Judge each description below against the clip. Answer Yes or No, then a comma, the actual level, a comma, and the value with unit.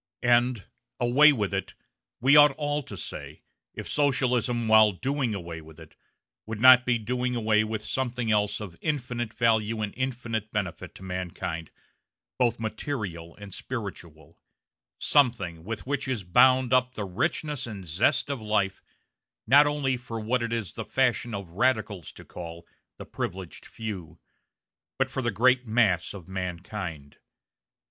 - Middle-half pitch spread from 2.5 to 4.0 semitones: No, average, 5.0 semitones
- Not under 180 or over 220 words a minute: No, average, 150 wpm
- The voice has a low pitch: Yes, low, 110 Hz